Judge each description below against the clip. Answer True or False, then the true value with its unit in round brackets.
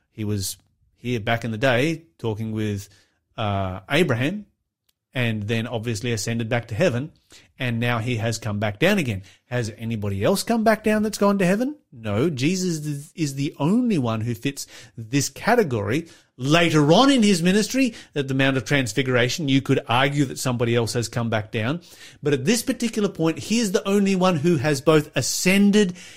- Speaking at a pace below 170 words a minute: False (185 wpm)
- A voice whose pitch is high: False (135 Hz)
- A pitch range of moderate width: False (7.2 semitones)